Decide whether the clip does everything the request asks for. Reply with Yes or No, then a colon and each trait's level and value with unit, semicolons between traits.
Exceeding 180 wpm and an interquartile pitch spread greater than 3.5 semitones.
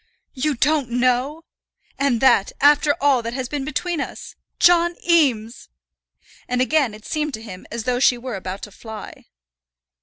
No: average, 160 wpm; average, 4.2 semitones